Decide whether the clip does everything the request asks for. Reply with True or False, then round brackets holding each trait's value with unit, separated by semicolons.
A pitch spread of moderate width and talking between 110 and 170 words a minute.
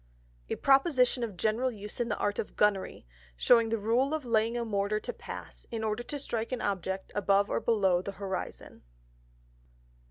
False (3.1 semitones; 180 wpm)